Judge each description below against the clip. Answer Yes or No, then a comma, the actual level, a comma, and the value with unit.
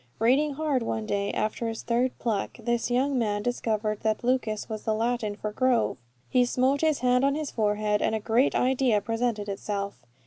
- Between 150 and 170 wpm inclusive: No, average, 185 wpm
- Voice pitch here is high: Yes, high, 230 Hz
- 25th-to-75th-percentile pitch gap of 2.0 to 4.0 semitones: Yes, average, 3.0 semitones